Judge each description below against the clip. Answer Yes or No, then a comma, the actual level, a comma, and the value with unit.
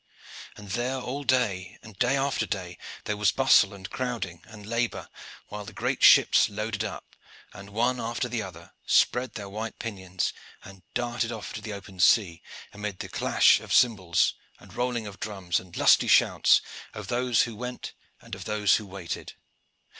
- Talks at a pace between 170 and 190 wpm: Yes, average, 175 wpm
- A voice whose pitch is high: No, low, 105 Hz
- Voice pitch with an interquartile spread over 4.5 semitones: No, average, 3.7 semitones